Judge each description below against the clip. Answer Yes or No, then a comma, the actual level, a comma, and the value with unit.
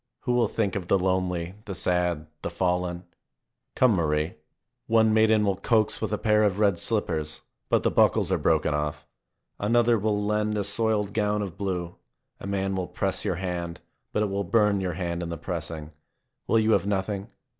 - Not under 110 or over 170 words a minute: No, average, 190 wpm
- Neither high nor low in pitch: No, very low, 95 Hz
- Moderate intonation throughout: Yes, average, 3.4 semitones